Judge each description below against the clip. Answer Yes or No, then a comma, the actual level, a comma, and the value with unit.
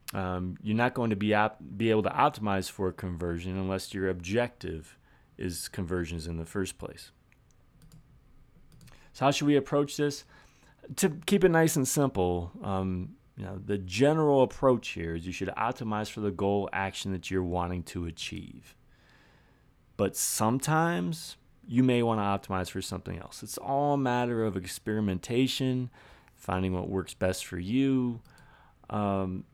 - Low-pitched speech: Yes, low, 100 Hz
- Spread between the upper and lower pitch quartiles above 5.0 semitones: Yes, wide, 5.6 semitones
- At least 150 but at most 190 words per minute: Yes, average, 160 wpm